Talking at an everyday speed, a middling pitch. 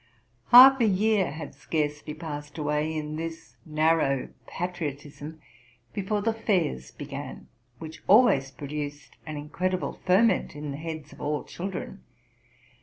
No: slow, 125 wpm; medium, 155 Hz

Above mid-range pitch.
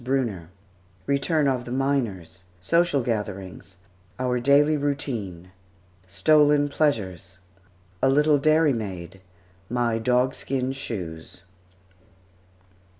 No: low, 125 Hz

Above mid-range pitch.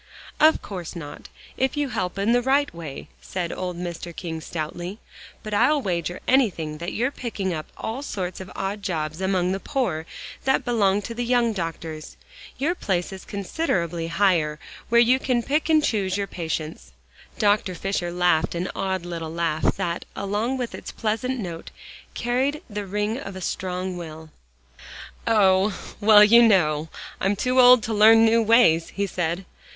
Yes: high, 195 Hz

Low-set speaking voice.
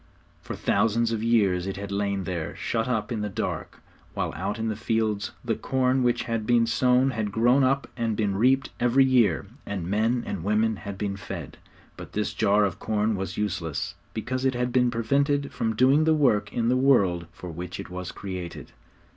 Yes: low, 110 Hz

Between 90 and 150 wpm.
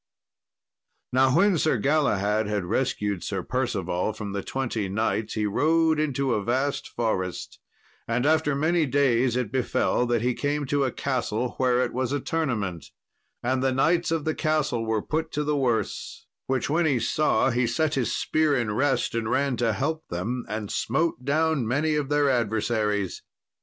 No: average, 170 wpm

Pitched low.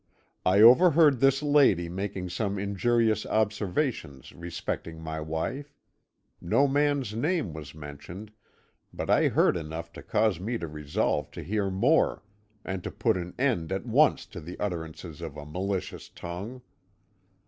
Yes: very low, 95 Hz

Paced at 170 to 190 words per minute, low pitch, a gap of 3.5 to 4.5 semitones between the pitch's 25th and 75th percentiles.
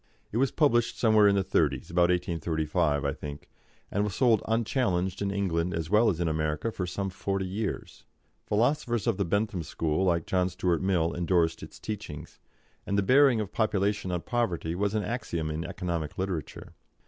Yes: average, 180 wpm; very low, 95 Hz; average, 4.2 semitones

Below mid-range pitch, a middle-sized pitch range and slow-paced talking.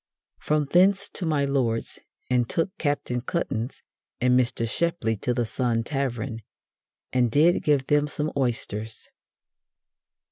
Yes: low, 130 Hz; average, 4.2 semitones; slow, 130 wpm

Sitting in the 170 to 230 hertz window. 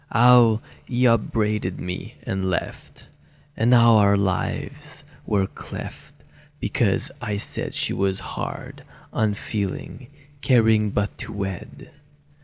No: low, 105 Hz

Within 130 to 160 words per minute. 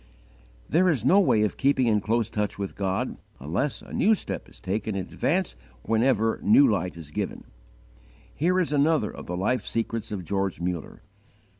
No: average, 175 wpm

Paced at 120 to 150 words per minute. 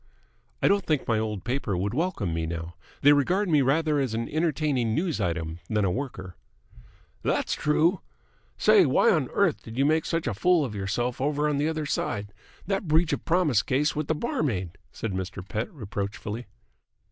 No: average, 185 wpm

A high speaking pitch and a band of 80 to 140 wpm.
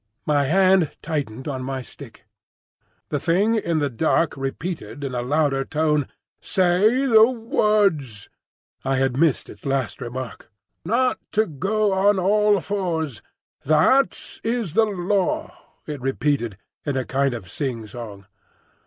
No: medium, 155 Hz; slow, 135 wpm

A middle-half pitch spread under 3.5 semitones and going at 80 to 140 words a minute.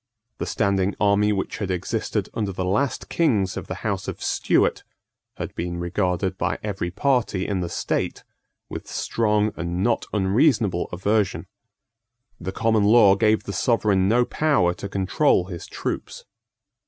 No: average, 2.9 semitones; average, 150 wpm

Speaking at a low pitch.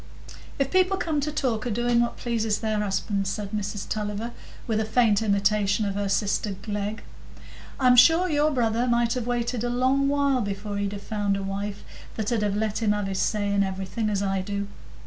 No: high, 215 Hz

